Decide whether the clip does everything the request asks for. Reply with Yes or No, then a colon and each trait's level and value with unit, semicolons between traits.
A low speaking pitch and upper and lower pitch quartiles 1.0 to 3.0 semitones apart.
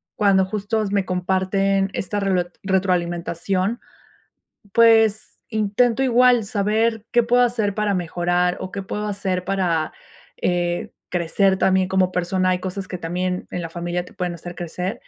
No: high, 190 Hz; average, 2.7 semitones